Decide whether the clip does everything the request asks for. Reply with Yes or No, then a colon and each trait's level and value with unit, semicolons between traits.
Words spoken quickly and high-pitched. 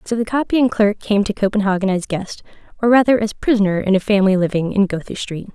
Yes: fast, 215 wpm; high, 205 Hz